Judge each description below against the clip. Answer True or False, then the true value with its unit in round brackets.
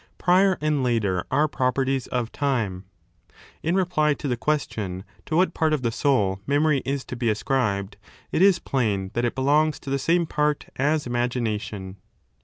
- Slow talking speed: False (170 wpm)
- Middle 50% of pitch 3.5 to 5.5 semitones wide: True (5.2 semitones)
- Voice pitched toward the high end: False (135 Hz)